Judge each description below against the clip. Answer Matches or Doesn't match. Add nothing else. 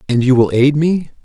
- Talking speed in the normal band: Doesn't match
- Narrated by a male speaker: Matches